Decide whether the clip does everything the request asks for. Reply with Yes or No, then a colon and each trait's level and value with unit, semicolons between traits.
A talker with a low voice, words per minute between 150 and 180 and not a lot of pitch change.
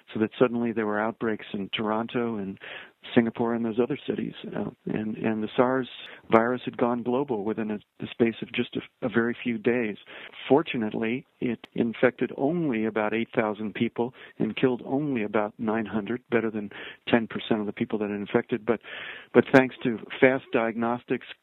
Yes: low, 115 Hz; average, 170 wpm; narrow, 2.0 semitones